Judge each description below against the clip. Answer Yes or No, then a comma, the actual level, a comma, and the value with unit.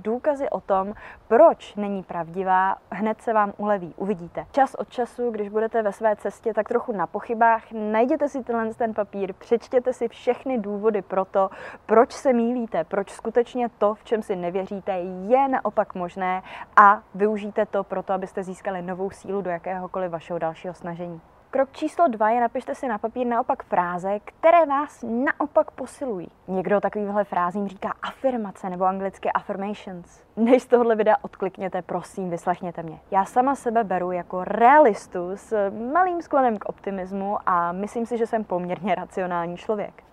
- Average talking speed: Yes, average, 160 wpm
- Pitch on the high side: Yes, high, 210 Hz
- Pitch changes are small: No, average, 3.9 semitones